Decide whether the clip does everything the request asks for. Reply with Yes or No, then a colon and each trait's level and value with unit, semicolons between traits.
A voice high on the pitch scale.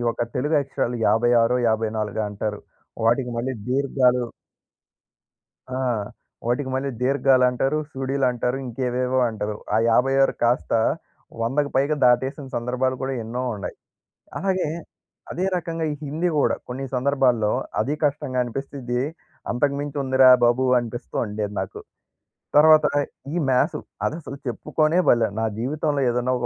No: low, 130 Hz